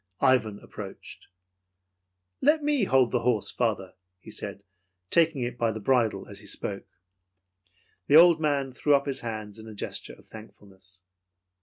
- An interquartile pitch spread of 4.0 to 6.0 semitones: Yes, average, 5.0 semitones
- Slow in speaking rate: No, average, 155 wpm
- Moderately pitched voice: No, low, 120 Hz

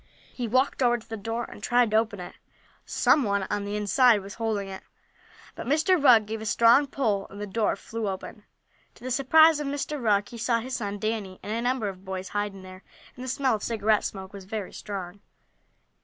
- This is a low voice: No, high, 220 Hz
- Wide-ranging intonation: No, average, 3.5 semitones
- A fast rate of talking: Yes, fast, 215 wpm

